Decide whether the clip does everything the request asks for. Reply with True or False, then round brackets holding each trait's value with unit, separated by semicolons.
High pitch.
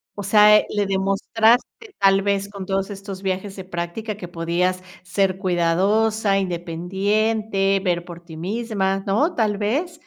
True (195 Hz)